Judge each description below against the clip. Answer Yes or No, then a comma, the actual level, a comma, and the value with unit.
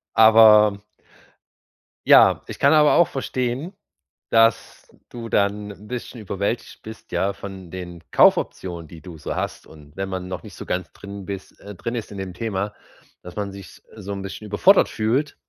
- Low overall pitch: Yes, low, 100 Hz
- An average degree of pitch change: Yes, average, 3.3 semitones